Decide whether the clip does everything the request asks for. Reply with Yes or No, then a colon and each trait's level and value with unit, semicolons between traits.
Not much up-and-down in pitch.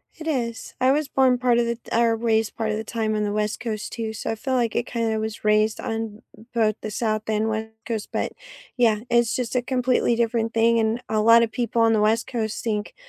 Yes: narrow, 1.5 semitones